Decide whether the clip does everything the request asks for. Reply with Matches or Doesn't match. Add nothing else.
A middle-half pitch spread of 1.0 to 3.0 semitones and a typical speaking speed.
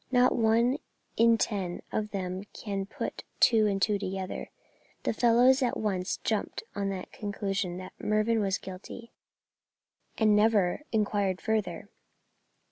Doesn't match